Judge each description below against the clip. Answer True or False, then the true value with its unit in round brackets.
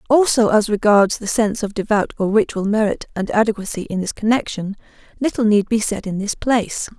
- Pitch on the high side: True (215 Hz)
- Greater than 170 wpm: True (190 wpm)